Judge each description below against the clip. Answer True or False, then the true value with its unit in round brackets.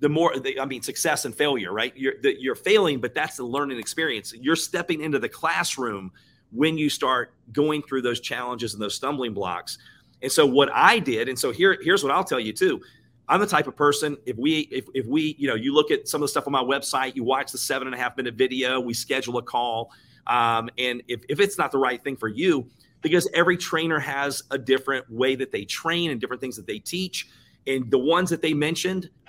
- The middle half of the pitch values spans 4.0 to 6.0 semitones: True (5.0 semitones)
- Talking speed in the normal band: False (235 wpm)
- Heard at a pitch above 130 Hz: True (140 Hz)